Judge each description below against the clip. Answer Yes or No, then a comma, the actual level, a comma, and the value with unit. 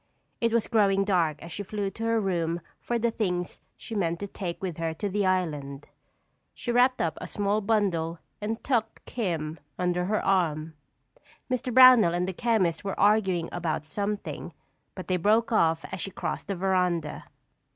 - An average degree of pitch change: Yes, average, 4.2 semitones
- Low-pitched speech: No, high, 190 Hz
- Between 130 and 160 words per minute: No, average, 175 wpm